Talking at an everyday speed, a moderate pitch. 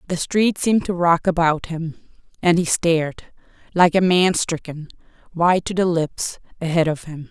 Yes: average, 165 wpm; medium, 170 Hz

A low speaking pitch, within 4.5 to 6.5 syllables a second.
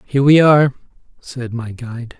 Yes: low, 130 Hz; 5.5 syllables/s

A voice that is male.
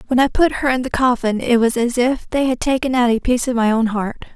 No: female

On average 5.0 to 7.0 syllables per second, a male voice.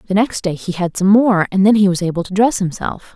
No: 5.8 syllables/s; female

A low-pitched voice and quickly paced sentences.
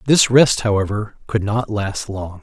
No: low, 105 Hz; average, 175 wpm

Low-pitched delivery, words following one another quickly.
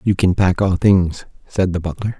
Yes: very low, 90 Hz; fast, 220 wpm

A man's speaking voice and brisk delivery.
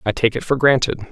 Yes: male; fast, 270 wpm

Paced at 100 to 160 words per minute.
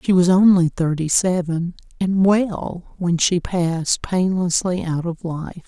Yes: average, 150 wpm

